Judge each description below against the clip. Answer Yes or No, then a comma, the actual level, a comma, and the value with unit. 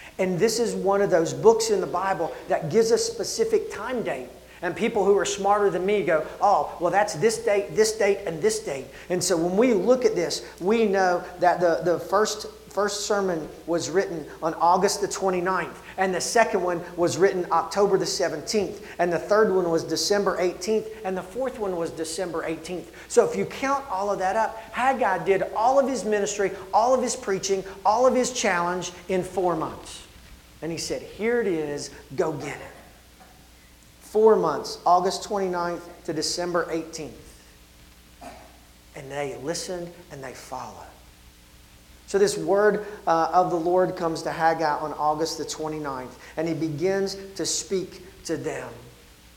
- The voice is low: No, medium, 185 Hz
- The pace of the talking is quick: No, average, 175 wpm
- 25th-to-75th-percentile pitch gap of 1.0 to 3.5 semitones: No, average, 4.2 semitones